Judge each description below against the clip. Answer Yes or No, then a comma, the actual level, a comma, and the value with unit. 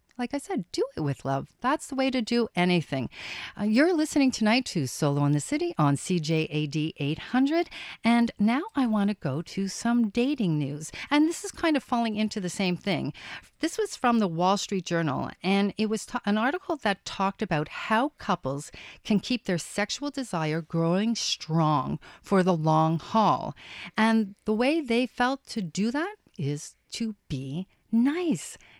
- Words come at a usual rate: Yes, average, 180 wpm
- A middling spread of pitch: No, wide, 7.2 semitones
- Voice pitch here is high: Yes, high, 210 Hz